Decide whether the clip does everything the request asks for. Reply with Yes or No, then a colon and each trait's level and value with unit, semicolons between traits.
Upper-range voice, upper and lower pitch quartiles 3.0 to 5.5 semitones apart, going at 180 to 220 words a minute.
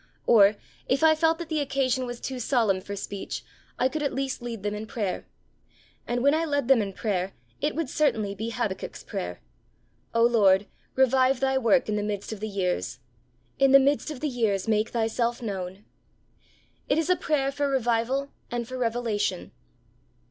Yes: high, 240 Hz; average, 4.7 semitones; average, 185 wpm